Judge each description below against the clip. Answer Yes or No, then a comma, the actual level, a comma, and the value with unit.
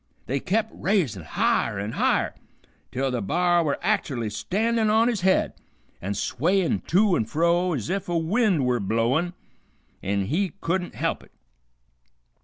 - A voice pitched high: No, medium, 170 Hz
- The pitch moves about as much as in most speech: No, wide, 8.0 semitones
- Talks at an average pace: Yes, average, 155 wpm